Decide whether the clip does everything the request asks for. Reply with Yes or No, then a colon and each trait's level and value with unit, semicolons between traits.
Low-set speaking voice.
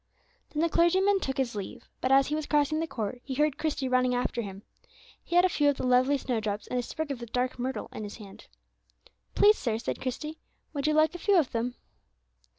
No: very high, 265 Hz